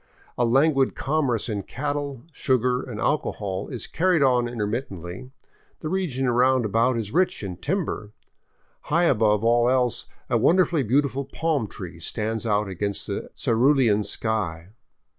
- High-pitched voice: No, low, 125 Hz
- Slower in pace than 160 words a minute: Yes, average, 140 wpm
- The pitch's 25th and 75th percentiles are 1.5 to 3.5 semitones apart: No, average, 5.0 semitones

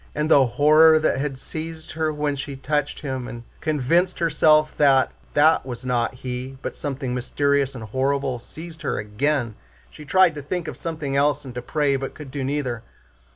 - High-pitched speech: No, medium, 140 Hz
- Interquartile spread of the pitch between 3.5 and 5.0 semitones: No, average, 2.9 semitones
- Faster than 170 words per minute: Yes, average, 185 wpm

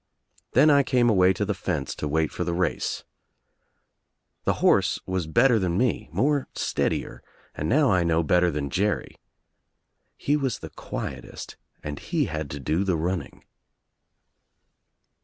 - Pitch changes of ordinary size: No, wide, 7.0 semitones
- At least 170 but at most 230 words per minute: No, average, 150 wpm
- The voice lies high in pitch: No, very low, 90 Hz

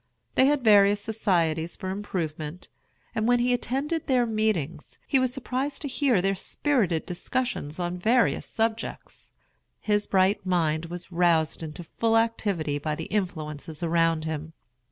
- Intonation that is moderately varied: No, wide, 6.0 semitones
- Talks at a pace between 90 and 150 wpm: Yes, average, 145 wpm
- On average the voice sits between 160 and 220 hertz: Yes, high, 190 Hz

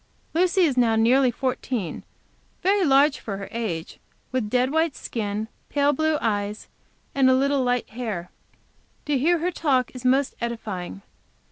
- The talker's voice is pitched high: Yes, very high, 255 Hz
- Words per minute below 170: Yes, average, 155 wpm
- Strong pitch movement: No, average, 4.4 semitones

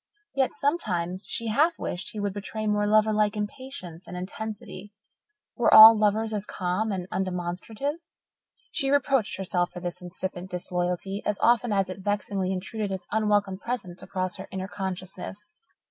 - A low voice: No, high, 200 Hz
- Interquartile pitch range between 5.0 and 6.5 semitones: No, average, 2.9 semitones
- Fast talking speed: No, average, 155 wpm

